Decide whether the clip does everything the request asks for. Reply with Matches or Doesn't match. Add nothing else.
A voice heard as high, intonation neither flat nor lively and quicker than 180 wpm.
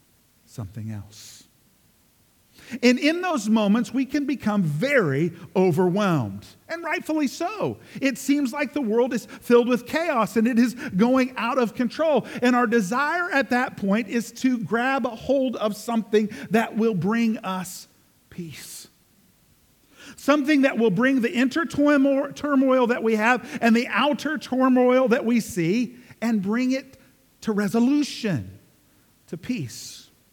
Doesn't match